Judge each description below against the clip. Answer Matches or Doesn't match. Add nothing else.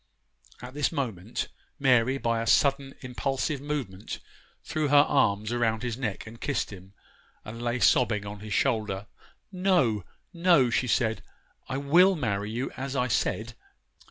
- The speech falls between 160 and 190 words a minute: Doesn't match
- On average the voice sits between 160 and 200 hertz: Doesn't match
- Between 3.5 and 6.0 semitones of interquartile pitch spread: Matches